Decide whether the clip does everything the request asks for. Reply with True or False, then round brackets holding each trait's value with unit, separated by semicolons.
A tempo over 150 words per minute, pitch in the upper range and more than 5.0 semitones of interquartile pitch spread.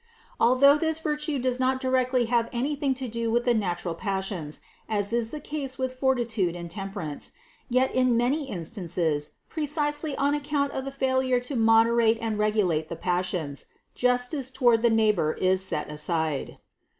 True (165 wpm; 235 Hz; 5.5 semitones)